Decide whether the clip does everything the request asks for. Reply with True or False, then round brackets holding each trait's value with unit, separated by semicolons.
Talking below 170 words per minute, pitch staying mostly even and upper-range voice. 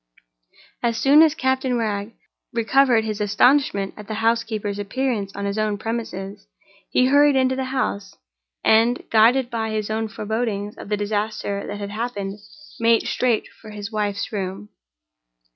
False (150 wpm; 3.1 semitones; 220 Hz)